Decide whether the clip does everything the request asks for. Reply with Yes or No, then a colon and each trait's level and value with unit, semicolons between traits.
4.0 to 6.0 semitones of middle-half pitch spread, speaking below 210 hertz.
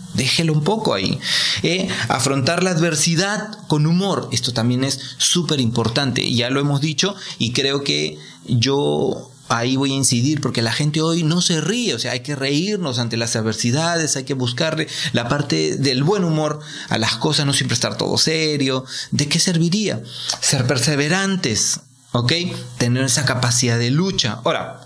Yes: average, 5.0 semitones; medium, 140 Hz